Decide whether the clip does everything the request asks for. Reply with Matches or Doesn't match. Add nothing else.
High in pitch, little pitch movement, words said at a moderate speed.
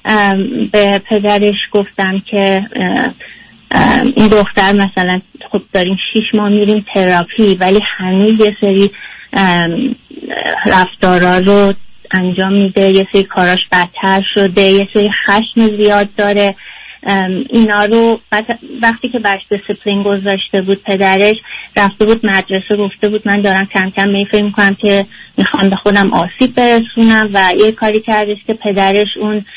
Matches